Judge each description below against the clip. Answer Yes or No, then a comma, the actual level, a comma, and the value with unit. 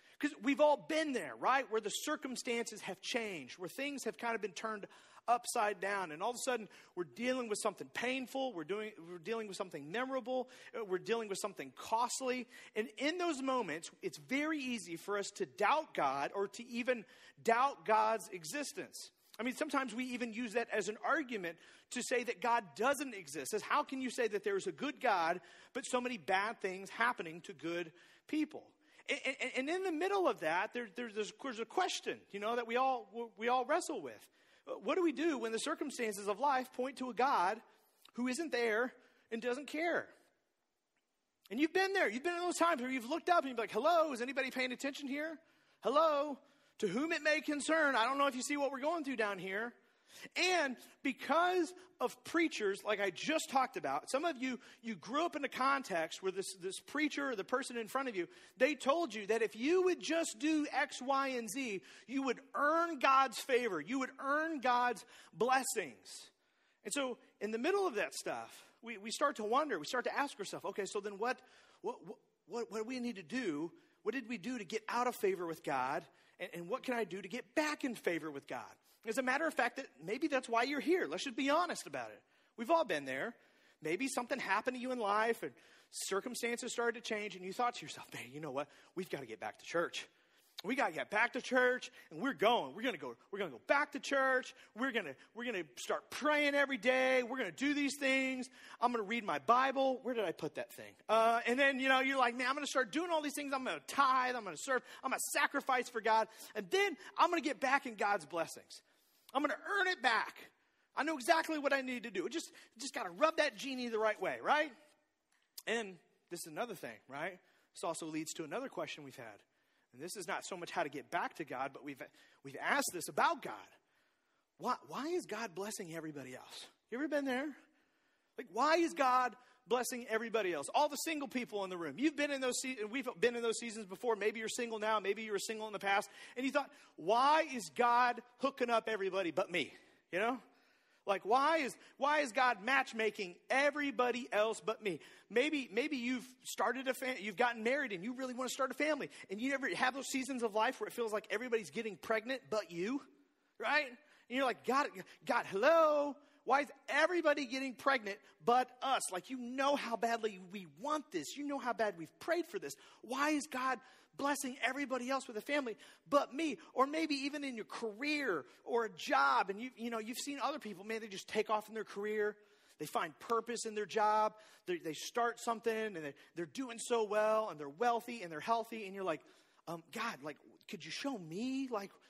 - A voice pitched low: No, very high, 250 Hz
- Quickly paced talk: Yes, fast, 225 wpm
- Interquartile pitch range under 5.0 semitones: Yes, average, 4.5 semitones